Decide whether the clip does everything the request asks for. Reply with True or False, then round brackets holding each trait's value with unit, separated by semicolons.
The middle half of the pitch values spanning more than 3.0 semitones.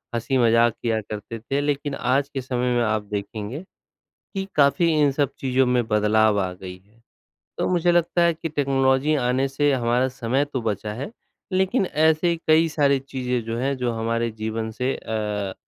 True (4.2 semitones)